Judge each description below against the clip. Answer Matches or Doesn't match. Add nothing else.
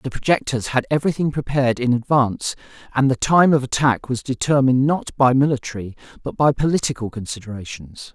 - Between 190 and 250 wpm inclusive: Doesn't match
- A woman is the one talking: Doesn't match